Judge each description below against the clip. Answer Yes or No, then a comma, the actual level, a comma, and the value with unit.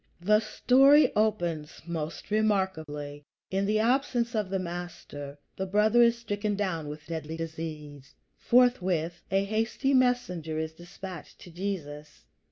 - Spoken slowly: Yes, slow, 130 wpm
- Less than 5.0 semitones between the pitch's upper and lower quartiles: No, average, 5.3 semitones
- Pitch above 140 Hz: Yes, medium, 185 Hz